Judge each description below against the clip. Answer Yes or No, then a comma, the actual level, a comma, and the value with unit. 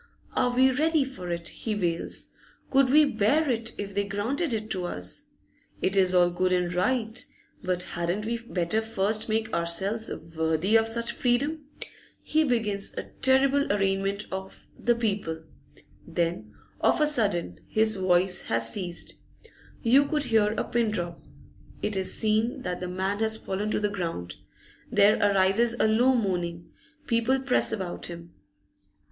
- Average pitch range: Yes, average, 4.6 semitones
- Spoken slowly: No, average, 155 wpm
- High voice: Yes, high, 205 Hz